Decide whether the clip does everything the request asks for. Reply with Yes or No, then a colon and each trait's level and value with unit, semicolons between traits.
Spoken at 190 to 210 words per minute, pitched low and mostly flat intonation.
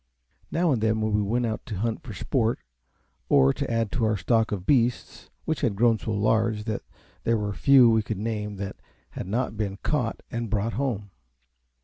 Yes: average, 195 wpm; low, 110 Hz; narrow, 2.1 semitones